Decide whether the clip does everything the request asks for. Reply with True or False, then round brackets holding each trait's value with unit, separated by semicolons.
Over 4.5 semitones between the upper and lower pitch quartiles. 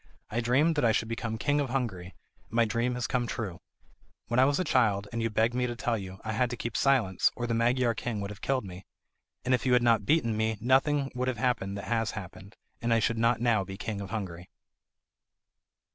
False (2.9 semitones)